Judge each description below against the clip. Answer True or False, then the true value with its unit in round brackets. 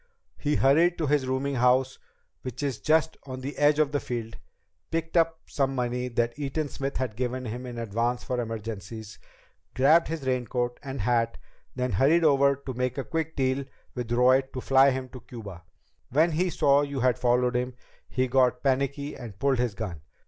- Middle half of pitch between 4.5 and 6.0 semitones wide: False (2.5 semitones)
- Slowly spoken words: False (185 wpm)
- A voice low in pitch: True (130 Hz)